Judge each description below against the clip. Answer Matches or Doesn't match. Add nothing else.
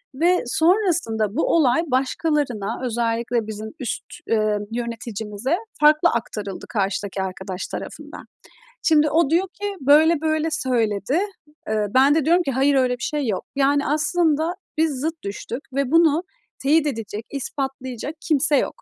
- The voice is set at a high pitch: Matches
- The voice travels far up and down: Matches